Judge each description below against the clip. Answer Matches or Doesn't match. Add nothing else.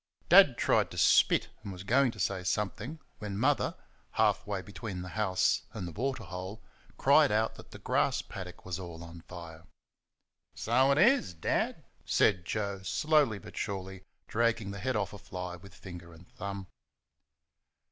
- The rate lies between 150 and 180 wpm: Matches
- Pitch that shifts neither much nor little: Matches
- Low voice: Matches